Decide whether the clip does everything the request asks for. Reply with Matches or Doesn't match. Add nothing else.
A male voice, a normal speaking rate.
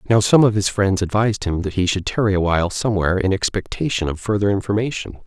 Doesn't match